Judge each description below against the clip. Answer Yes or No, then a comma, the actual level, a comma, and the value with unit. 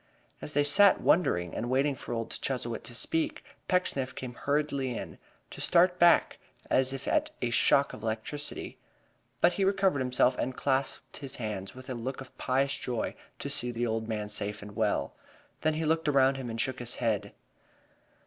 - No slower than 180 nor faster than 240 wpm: Yes, average, 185 wpm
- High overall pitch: No, low, 130 Hz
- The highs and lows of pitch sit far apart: No, average, 3.8 semitones